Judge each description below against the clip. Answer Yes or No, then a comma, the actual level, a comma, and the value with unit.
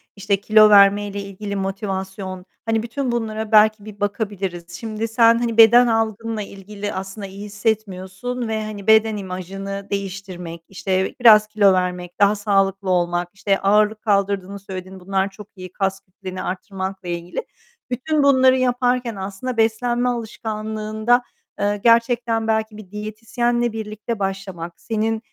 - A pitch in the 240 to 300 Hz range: No, high, 205 Hz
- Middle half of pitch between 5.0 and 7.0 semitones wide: No, narrow, 2.5 semitones